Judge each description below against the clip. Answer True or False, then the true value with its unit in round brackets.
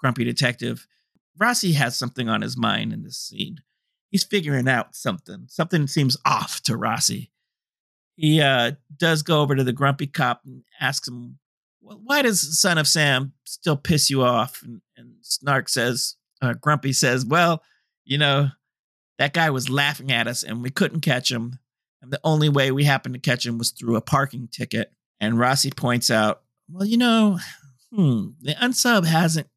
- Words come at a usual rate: True (180 wpm)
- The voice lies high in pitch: False (140 Hz)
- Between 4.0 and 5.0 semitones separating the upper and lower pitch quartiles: True (4.3 semitones)